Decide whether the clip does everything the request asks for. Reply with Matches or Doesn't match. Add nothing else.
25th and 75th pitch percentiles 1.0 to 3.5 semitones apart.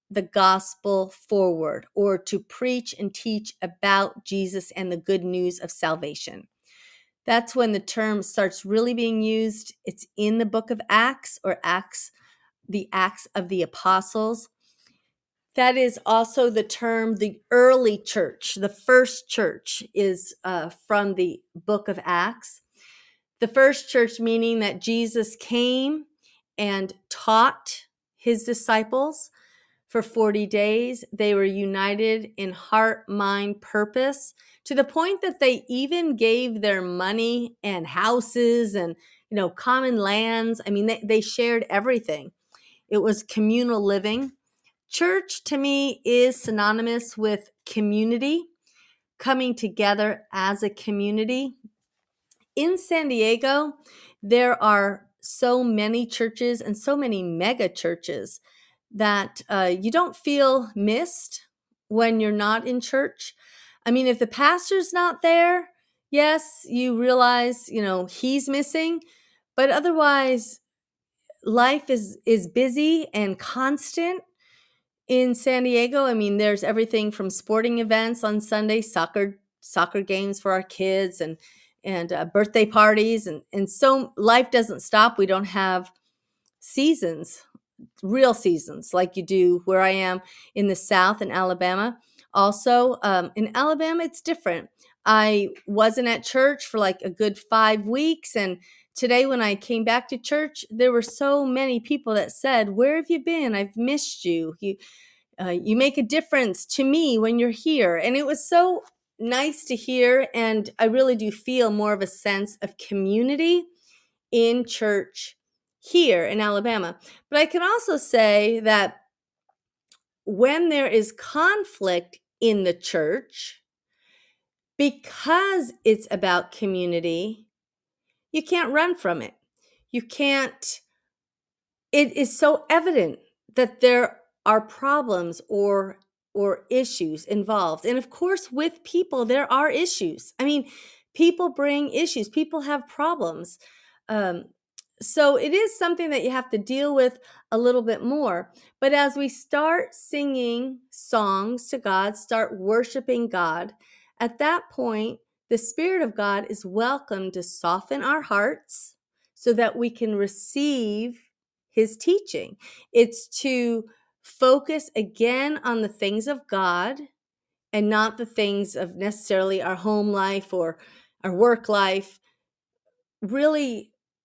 Doesn't match